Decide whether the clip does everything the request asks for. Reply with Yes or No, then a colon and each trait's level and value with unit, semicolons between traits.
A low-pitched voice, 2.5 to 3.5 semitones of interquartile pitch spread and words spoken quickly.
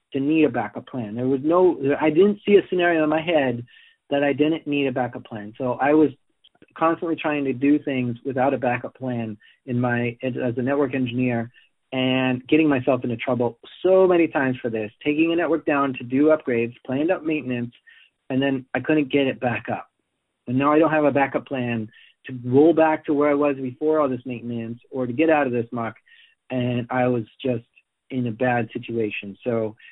No: low, 130 Hz; average, 3.9 semitones; fast, 210 wpm